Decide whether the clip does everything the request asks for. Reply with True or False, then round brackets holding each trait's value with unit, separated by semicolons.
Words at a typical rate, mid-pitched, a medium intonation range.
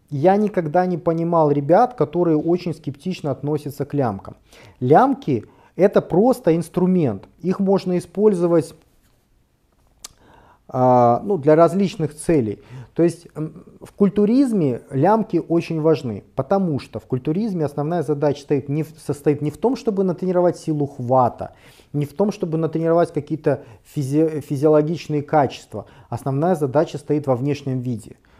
True (135 wpm; 155 Hz; 4.1 semitones)